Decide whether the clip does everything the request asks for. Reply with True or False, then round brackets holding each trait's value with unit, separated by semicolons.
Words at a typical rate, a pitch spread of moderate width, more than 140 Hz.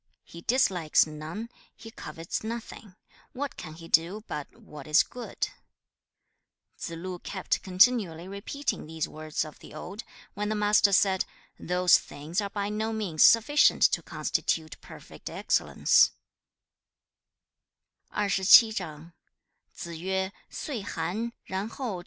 False (110 wpm; 5.0 semitones; 190 Hz)